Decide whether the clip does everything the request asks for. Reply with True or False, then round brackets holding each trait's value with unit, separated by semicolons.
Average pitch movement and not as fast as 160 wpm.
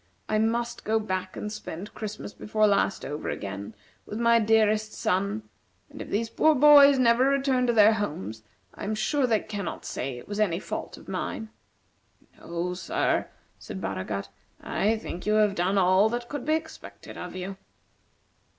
False (4.1 semitones; 170 wpm)